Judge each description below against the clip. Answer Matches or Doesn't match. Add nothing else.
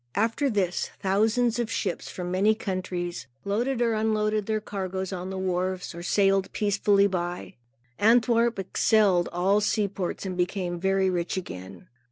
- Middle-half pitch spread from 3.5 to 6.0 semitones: Doesn't match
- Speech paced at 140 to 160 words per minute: Matches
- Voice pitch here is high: Matches